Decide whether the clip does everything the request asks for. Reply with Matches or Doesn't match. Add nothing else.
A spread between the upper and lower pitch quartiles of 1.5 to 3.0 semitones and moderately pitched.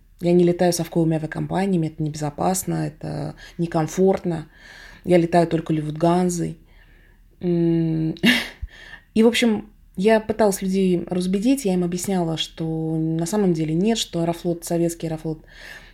Matches